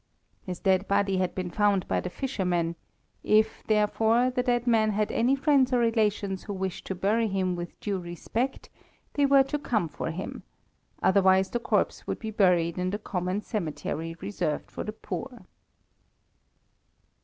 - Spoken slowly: No, average, 165 wpm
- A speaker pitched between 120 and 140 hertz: No, high, 205 Hz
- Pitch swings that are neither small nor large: Yes, average, 3.9 semitones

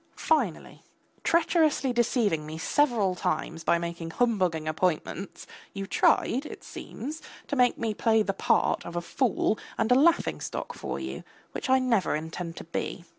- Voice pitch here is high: Yes, high, 210 Hz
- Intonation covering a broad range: Yes, wide, 6.9 semitones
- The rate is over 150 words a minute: Yes, average, 160 wpm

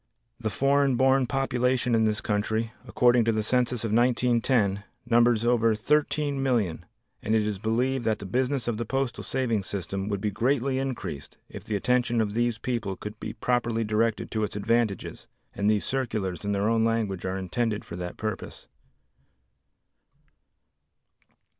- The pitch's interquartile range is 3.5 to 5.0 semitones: No, average, 3.0 semitones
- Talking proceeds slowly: No, average, 160 wpm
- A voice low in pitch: Yes, low, 115 Hz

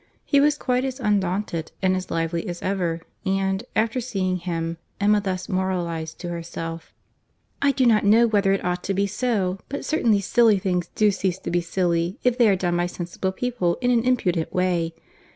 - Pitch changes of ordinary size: Yes, average, 3.9 semitones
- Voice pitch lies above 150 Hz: Yes, high, 190 Hz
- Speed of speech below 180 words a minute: No, average, 190 wpm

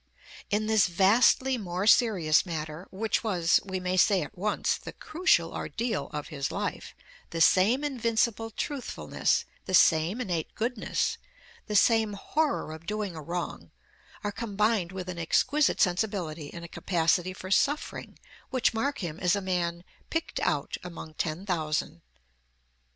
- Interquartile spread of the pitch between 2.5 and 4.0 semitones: No, average, 4.7 semitones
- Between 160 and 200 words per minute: No, average, 145 wpm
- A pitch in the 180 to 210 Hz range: Yes, high, 190 Hz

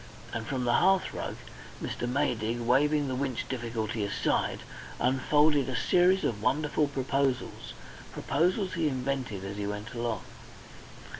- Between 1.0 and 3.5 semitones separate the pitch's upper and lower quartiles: No, average, 4.0 semitones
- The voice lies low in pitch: Yes, low, 130 Hz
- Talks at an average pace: No, slow, 130 wpm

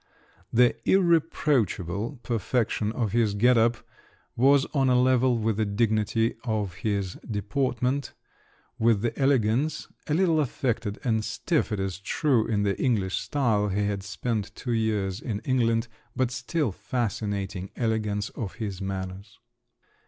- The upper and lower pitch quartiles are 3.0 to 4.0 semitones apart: Yes, average, 3.6 semitones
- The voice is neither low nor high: No, low, 115 Hz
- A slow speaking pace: Yes, slow, 130 wpm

